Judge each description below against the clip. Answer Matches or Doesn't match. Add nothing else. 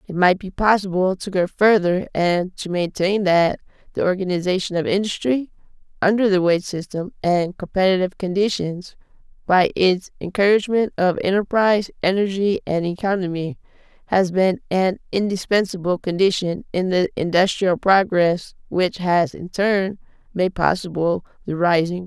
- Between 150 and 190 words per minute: Doesn't match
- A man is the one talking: Doesn't match